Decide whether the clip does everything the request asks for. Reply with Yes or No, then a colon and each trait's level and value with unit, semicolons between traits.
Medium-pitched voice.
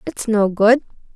No: high, 225 Hz